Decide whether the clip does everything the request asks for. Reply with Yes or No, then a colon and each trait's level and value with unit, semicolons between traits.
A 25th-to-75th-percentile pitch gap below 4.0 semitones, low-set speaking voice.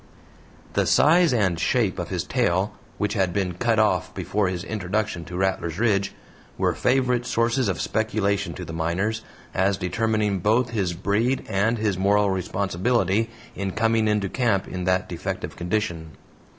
Yes: average, 3.3 semitones; low, 100 Hz